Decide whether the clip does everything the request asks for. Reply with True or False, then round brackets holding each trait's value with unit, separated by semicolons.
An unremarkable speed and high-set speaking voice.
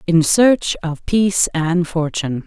False (145 wpm; 170 Hz)